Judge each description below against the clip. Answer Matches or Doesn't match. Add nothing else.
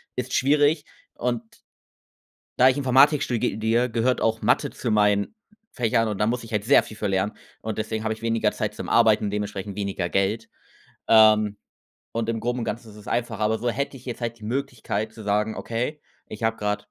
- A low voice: Matches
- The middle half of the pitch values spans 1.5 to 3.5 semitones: Matches